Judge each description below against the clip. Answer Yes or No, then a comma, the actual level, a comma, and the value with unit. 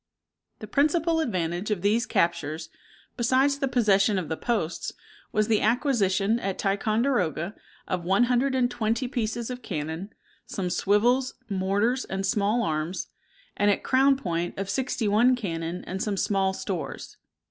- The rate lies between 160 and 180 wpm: No, average, 145 wpm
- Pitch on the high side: Yes, high, 210 Hz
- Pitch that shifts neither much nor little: Yes, average, 4.8 semitones